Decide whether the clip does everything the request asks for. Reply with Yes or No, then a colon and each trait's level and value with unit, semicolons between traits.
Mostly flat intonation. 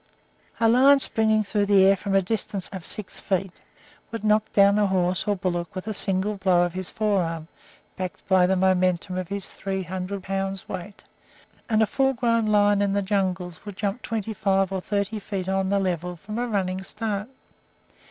Yes: narrow, 2.1 semitones